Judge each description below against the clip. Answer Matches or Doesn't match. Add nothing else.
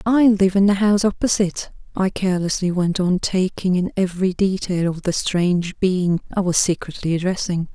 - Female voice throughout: Matches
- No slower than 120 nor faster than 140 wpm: Doesn't match